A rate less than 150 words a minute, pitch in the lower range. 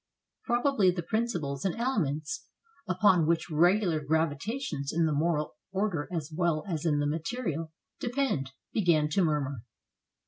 No: slow, 135 wpm; medium, 165 Hz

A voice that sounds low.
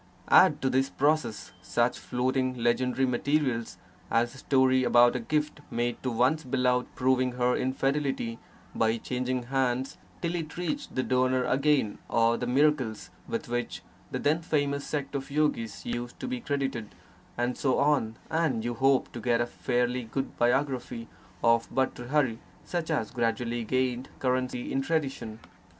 Yes: low, 130 Hz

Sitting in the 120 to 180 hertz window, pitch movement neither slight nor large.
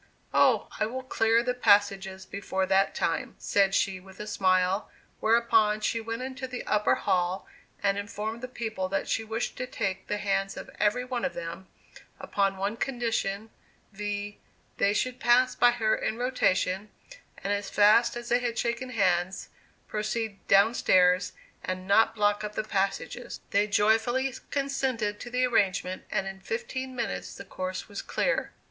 No: high, 210 Hz; average, 3.5 semitones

